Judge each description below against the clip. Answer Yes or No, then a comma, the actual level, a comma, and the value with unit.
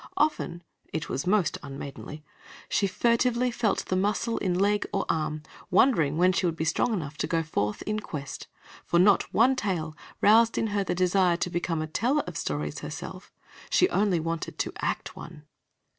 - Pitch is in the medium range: Yes, medium, 180 Hz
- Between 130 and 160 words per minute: No, average, 185 wpm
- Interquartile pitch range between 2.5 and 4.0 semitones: No, average, 5.0 semitones